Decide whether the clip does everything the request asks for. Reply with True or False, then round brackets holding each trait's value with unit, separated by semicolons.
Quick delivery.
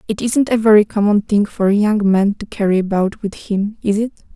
True (235 wpm)